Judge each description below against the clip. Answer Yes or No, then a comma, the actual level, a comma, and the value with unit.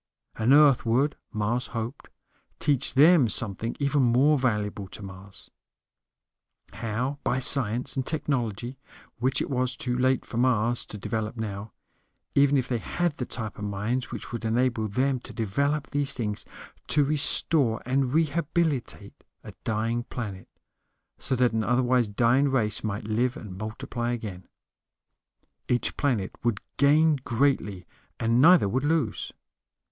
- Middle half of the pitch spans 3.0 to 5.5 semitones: Yes, average, 4.0 semitones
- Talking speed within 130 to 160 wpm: Yes, average, 140 wpm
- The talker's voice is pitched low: Yes, low, 125 Hz